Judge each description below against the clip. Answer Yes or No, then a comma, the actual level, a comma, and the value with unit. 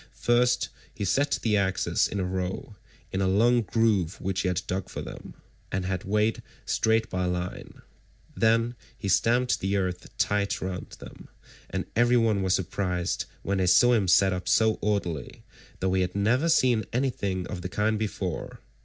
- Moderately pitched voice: No, low, 100 Hz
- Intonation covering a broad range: No, average, 3.4 semitones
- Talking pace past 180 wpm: No, average, 175 wpm